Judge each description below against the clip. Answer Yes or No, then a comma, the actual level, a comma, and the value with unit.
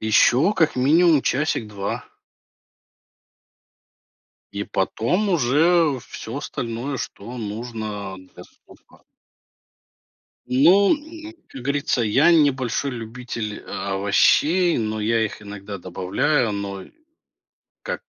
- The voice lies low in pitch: Yes, low, 120 Hz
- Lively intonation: Yes, wide, 6.5 semitones